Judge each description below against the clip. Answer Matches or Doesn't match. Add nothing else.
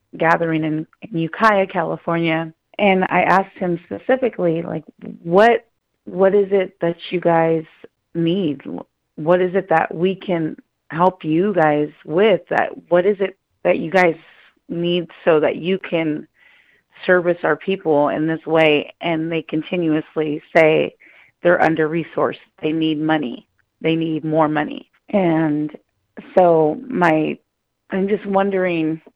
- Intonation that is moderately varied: Matches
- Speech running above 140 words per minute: Doesn't match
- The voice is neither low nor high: Matches